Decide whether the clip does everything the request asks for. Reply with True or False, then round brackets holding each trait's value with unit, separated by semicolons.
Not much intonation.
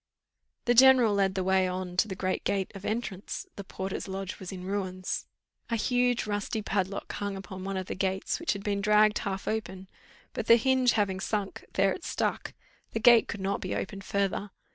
True (2.2 semitones)